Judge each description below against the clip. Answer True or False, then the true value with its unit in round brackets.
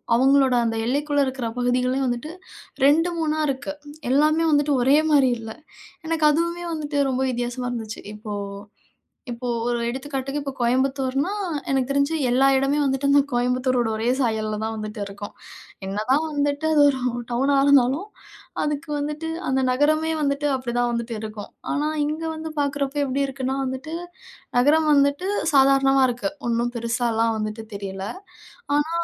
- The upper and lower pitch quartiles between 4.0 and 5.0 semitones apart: False (3.2 semitones)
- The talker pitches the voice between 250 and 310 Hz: True (270 Hz)